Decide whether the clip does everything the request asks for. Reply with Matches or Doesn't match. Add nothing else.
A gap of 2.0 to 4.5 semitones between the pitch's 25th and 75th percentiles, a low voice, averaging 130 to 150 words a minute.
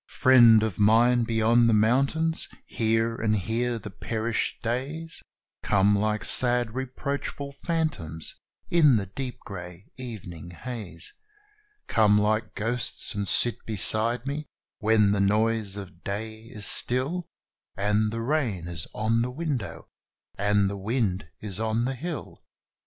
Matches